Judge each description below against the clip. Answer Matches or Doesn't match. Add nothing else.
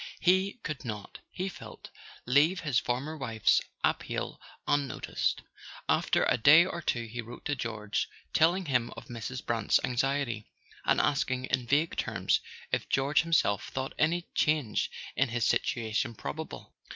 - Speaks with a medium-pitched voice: Doesn't match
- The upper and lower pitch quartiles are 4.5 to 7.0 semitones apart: Matches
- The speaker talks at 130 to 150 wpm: Matches